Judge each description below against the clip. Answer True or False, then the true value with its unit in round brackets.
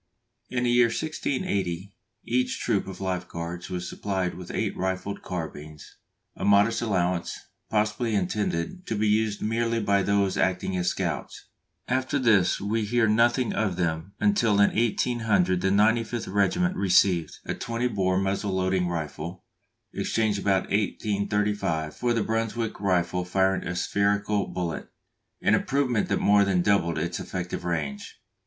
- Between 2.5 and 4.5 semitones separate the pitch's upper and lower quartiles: True (3.7 semitones)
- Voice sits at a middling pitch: False (100 Hz)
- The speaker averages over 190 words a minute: False (145 wpm)